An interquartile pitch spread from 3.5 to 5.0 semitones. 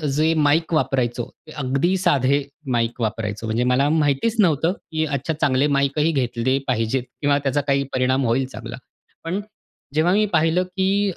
Yes: average, 4.0 semitones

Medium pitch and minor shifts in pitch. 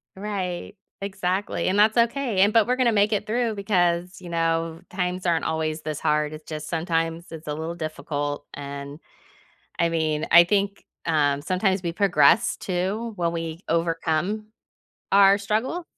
No: medium, 175 Hz; average, 4.0 semitones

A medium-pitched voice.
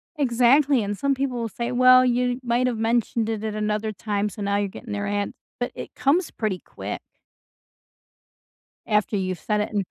No: high, 225 Hz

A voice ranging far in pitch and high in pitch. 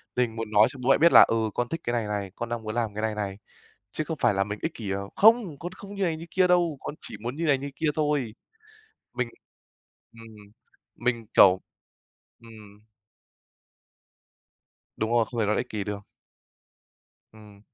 No: wide, 5.8 semitones; low, 115 Hz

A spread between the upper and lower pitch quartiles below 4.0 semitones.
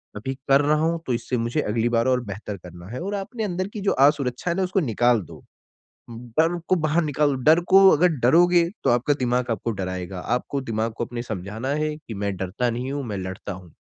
No: wide, 5.6 semitones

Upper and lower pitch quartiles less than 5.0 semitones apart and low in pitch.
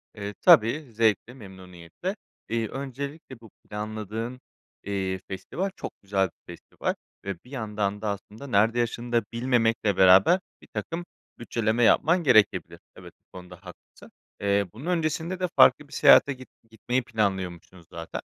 Yes: average, 4.5 semitones; low, 110 Hz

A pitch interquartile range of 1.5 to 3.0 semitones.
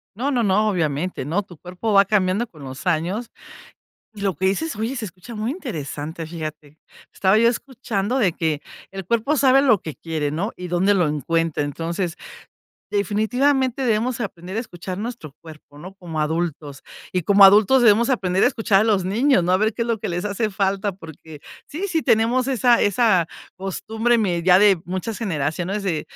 No: average, 5.0 semitones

